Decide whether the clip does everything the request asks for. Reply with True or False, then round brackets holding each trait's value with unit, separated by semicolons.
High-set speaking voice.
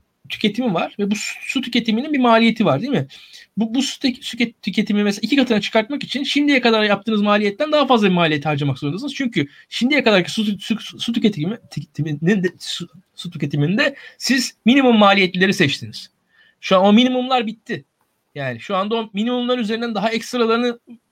True (220 Hz)